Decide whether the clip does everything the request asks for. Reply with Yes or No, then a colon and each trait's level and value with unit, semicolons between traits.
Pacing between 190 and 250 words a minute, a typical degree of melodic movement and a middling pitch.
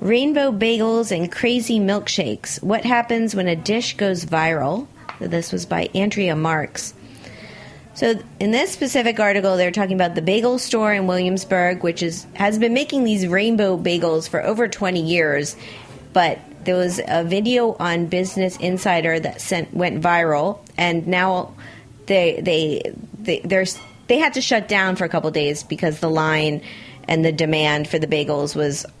No: average, 165 wpm; average, 4.3 semitones; medium, 180 Hz